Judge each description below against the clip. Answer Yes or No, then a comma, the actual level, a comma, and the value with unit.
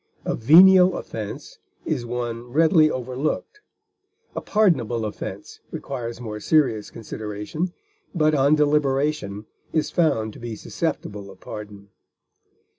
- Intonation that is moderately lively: No, wide, 6.0 semitones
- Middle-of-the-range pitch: No, low, 125 Hz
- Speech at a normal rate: No, slow, 115 wpm